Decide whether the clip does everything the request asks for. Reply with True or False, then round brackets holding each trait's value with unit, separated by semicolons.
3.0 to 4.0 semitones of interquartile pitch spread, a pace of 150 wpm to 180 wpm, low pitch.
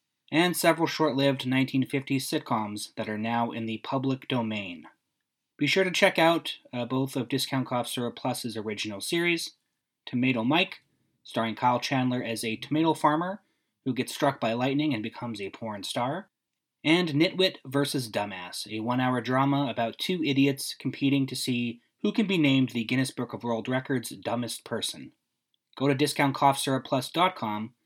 True (3.5 semitones; 155 wpm; 130 Hz)